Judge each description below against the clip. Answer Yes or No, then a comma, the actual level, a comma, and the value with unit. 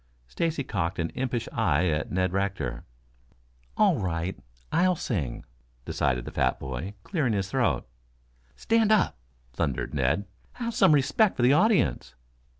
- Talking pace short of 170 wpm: Yes, average, 140 wpm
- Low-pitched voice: Yes, low, 100 Hz